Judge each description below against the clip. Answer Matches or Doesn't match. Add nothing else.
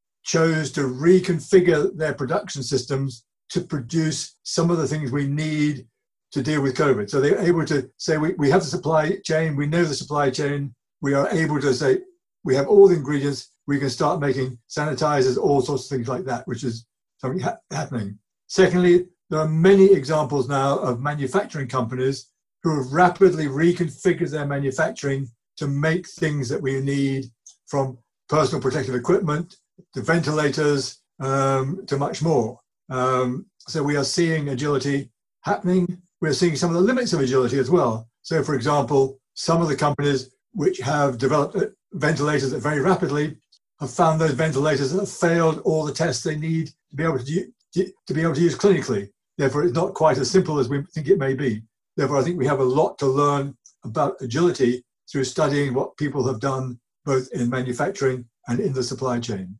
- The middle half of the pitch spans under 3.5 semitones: Doesn't match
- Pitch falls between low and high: Matches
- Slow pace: Doesn't match